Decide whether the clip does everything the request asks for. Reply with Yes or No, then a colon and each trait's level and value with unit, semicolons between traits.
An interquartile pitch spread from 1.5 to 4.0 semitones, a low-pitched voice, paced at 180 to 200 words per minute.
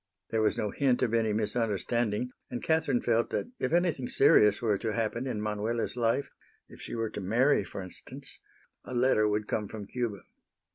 Yes: average, 2.7 semitones; low, 115 Hz; average, 185 wpm